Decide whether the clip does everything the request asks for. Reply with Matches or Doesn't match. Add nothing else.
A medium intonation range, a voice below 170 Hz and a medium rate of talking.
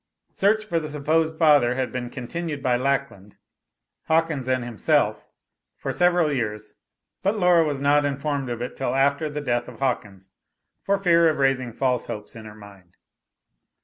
Matches